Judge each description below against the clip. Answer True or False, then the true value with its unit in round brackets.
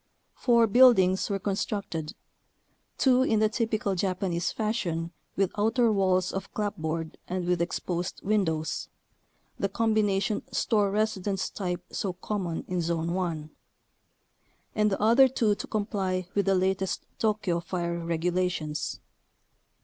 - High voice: True (195 Hz)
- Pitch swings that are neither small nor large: True (3.4 semitones)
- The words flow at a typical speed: False (125 wpm)